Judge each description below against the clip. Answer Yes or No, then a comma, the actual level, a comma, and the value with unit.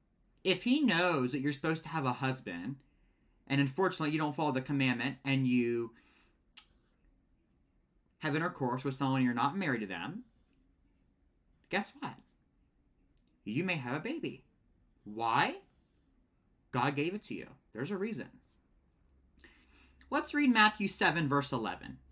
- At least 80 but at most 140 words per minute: Yes, slow, 135 wpm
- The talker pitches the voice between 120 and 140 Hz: Yes, low, 135 Hz